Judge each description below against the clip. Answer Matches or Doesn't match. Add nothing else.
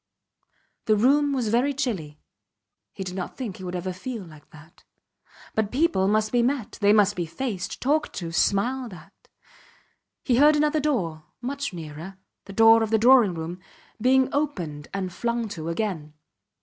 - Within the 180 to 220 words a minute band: Doesn't match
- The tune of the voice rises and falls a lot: Matches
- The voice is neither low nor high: Doesn't match